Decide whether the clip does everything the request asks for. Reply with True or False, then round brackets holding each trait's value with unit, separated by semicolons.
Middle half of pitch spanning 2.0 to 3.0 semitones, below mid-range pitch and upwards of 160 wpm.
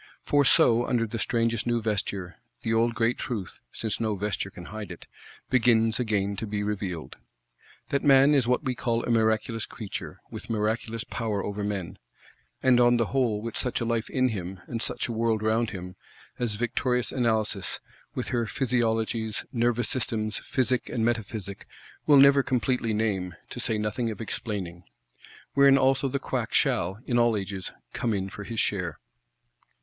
True (2.6 semitones; 115 Hz; 170 wpm)